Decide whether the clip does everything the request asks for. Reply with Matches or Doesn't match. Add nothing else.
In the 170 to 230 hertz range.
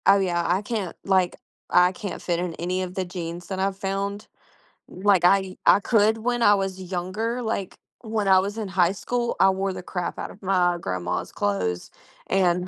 Matches